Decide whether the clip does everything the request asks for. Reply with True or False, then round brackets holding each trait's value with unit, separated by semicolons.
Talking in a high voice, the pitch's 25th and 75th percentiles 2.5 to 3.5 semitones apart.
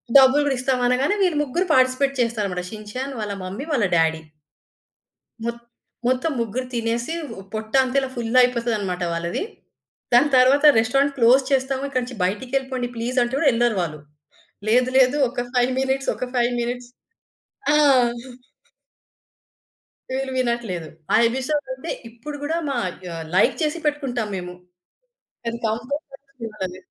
True (250 Hz; 3.1 semitones)